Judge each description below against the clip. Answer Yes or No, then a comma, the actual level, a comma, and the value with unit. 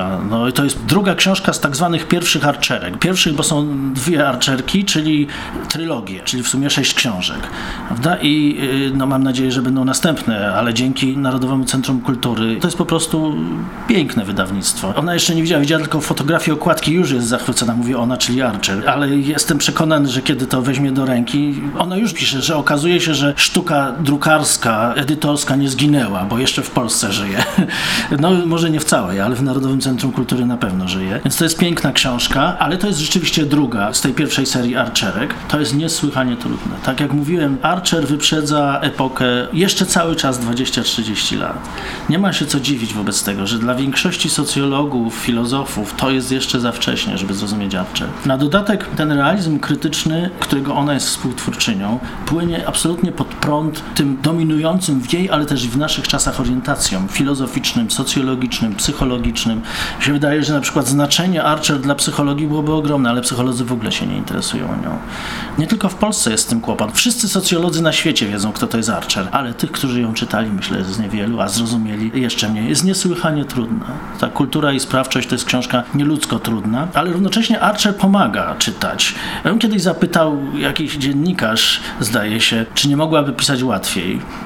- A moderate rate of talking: No, fast, 180 wpm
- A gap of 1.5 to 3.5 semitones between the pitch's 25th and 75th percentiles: No, average, 3.9 semitones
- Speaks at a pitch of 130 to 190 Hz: Yes, medium, 140 Hz